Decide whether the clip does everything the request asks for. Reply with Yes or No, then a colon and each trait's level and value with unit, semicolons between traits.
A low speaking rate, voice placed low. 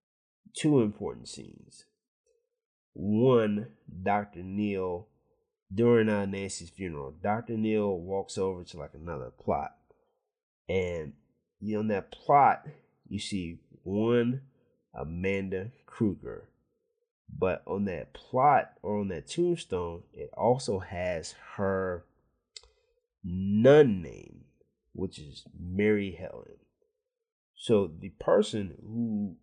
Yes: slow, 105 wpm; low, 105 Hz